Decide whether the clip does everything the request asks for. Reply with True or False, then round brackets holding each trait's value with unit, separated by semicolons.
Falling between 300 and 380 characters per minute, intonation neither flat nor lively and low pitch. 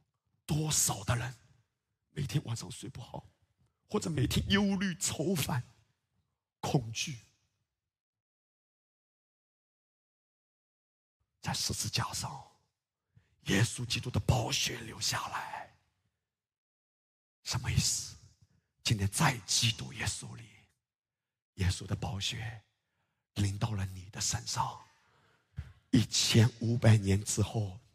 False (145 characters per minute; 3.5 semitones; 115 Hz)